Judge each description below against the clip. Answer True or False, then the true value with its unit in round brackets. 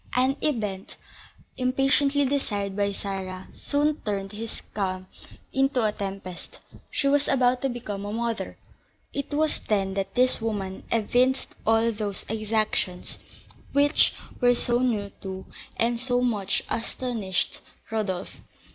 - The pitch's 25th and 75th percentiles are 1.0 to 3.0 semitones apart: False (4.3 semitones)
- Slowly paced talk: True (130 wpm)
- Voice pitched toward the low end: False (225 Hz)